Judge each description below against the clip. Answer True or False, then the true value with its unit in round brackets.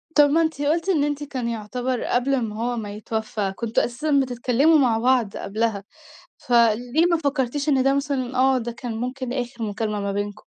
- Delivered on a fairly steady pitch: False (3.7 semitones)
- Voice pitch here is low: False (245 Hz)